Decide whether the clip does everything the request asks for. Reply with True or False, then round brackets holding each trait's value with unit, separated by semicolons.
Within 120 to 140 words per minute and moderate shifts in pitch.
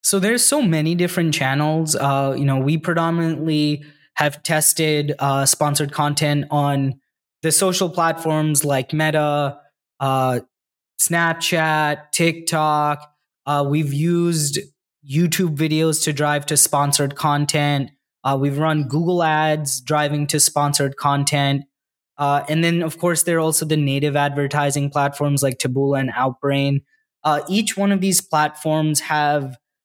False (135 wpm; 2.0 semitones)